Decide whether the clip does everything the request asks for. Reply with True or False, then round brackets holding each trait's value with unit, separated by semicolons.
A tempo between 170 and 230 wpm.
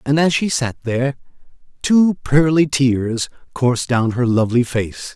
False (150 wpm)